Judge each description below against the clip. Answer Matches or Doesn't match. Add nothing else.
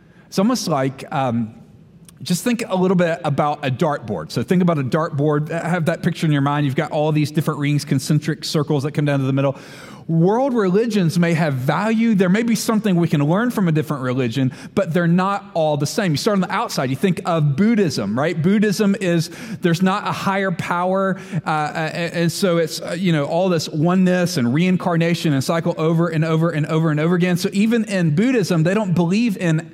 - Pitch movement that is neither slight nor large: Matches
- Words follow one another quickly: Matches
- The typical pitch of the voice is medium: Matches